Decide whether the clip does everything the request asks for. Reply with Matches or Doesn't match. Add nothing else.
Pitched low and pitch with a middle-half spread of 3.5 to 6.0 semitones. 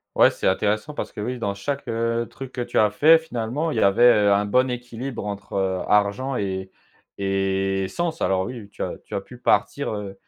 Matches